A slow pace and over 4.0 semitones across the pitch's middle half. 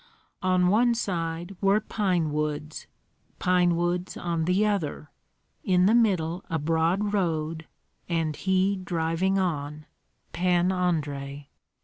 No: slow, 115 wpm; average, 2.9 semitones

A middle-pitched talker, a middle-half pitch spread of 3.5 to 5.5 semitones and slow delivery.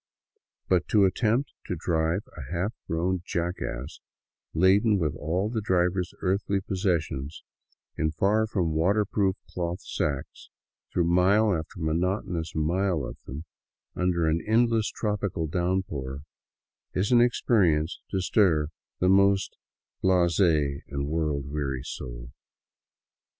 No: very low, 90 Hz; average, 4.0 semitones; slow, 120 wpm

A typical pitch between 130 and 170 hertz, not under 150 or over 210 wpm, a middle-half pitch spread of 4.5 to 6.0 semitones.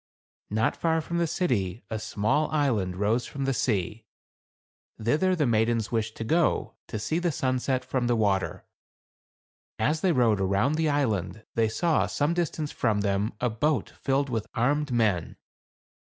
No: low, 120 Hz; average, 160 wpm; wide, 5.5 semitones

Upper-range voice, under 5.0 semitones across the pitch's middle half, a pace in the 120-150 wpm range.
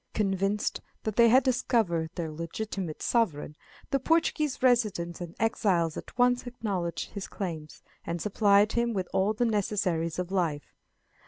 No: high, 200 Hz; wide, 5.4 semitones; average, 145 wpm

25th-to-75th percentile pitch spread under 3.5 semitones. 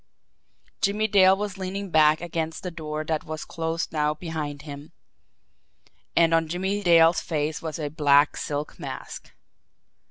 Yes: average, 2.9 semitones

